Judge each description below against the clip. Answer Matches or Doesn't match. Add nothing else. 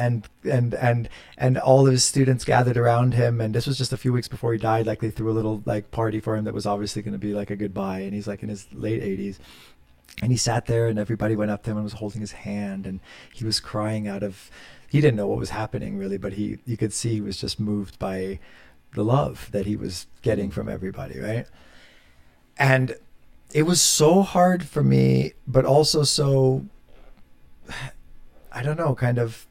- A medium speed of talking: Doesn't match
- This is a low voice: Matches